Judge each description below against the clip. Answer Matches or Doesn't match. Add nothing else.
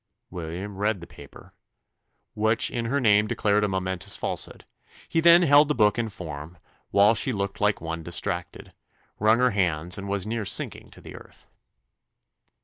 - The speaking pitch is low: Matches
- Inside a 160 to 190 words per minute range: Matches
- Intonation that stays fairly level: Doesn't match